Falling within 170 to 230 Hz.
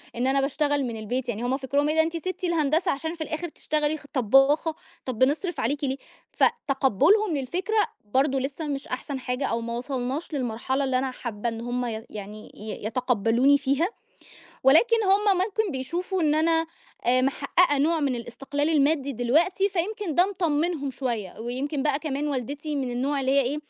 No: very high, 280 Hz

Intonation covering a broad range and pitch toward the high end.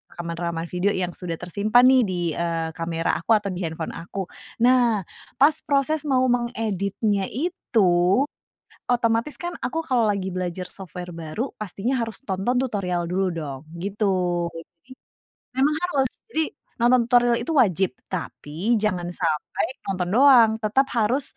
Yes: wide, 5.8 semitones; high, 200 Hz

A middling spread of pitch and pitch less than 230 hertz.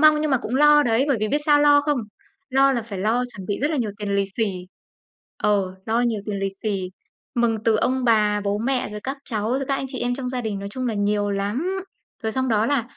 No: average, 4.4 semitones; high, 235 Hz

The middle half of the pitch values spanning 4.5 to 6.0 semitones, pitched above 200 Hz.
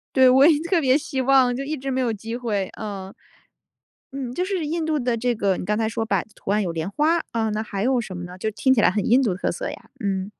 Yes: average, 4.8 semitones; high, 235 Hz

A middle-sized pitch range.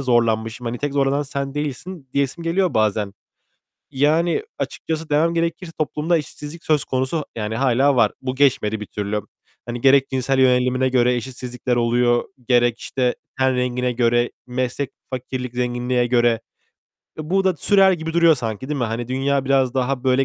Yes: average, 3.2 semitones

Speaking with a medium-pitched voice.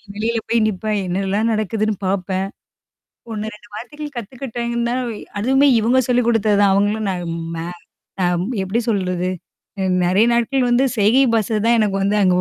No: high, 215 Hz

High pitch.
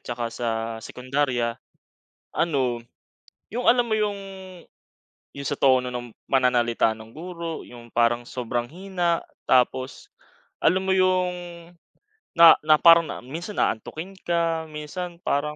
No: medium, 150 Hz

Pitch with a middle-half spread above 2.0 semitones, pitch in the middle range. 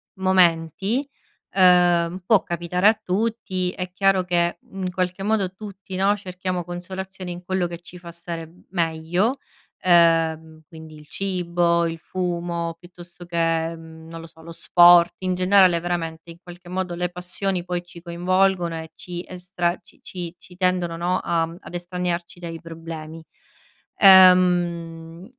No: narrow, 1.6 semitones; medium, 175 Hz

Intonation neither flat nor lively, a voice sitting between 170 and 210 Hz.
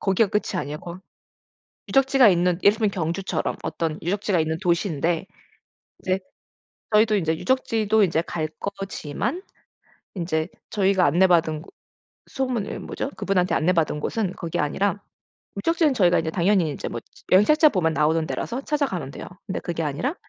Yes: average, 4.5 semitones; medium, 185 Hz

